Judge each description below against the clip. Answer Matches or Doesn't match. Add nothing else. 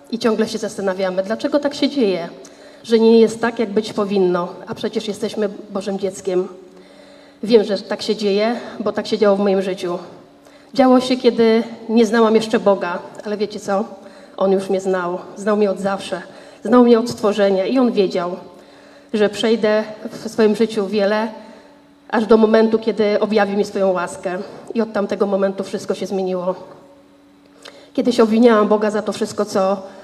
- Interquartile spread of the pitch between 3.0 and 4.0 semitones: Doesn't match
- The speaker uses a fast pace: Matches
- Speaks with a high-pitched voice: Matches